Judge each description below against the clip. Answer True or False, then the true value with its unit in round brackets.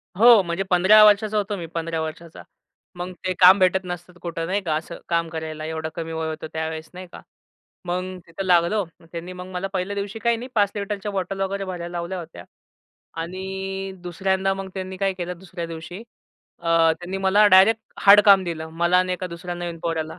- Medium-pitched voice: True (180 Hz)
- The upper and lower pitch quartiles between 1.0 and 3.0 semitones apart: True (2.4 semitones)